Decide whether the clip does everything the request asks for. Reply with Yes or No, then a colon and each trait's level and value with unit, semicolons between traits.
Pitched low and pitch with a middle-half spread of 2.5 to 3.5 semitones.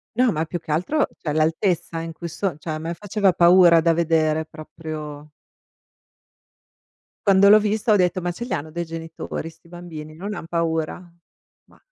No: medium, 165 Hz; average, 2.8 semitones